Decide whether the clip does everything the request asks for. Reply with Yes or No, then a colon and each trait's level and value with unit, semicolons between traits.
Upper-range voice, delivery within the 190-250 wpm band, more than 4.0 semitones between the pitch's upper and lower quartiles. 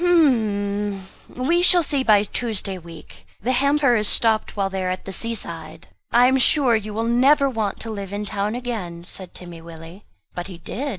Yes: high, 215 Hz; average, 195 wpm; average, 4.7 semitones